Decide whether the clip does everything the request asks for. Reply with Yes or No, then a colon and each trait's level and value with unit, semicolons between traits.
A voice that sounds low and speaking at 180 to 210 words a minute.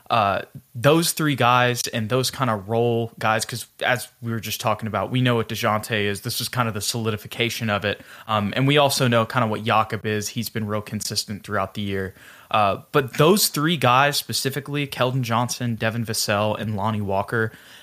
Yes: low, 115 Hz; average, 200 wpm